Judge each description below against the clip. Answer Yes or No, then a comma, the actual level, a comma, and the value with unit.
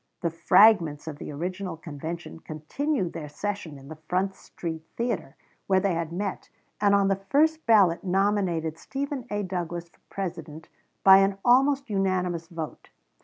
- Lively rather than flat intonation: No, average, 3.8 semitones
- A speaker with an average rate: Yes, average, 155 wpm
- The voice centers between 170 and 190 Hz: Yes, medium, 185 Hz